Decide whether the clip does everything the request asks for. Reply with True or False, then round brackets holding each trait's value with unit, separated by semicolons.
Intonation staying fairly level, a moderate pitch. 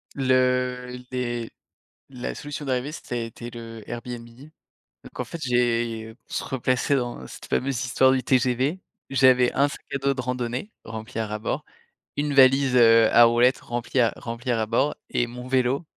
False (1.9 semitones; 125 Hz)